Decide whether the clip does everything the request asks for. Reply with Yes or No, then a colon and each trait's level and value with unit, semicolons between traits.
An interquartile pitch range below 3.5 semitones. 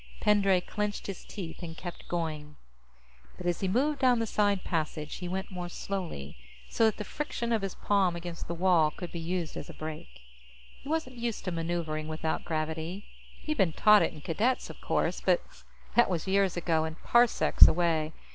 No: average, 4.3 semitones